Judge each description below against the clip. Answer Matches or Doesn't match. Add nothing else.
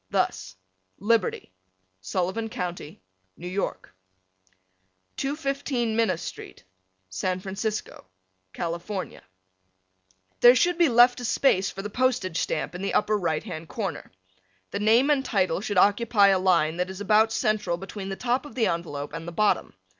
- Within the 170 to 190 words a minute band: Doesn't match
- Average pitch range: Matches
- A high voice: Matches